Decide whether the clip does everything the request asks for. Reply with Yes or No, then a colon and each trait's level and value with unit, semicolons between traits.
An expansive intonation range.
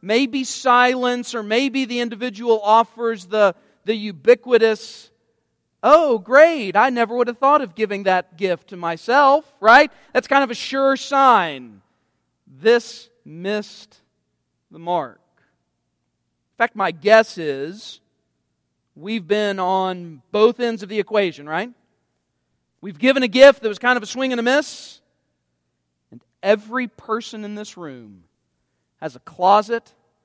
Yes: wide, 7.7 semitones